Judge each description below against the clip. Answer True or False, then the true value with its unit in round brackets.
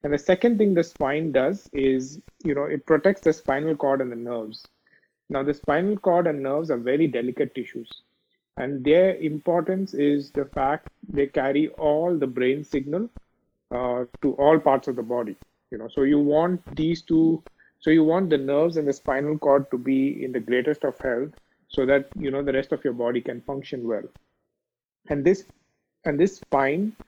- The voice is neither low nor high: True (145 Hz)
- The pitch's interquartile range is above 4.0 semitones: False (3.0 semitones)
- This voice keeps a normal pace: True (195 wpm)